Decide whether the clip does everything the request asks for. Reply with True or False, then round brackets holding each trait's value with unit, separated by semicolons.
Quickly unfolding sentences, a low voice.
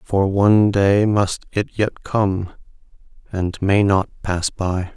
False (145 wpm; 100 Hz)